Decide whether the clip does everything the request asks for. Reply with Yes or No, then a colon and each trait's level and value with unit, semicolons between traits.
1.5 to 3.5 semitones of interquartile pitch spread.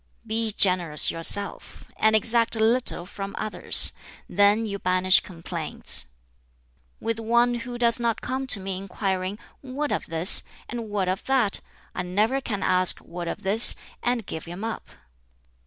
No: average, 4.0 semitones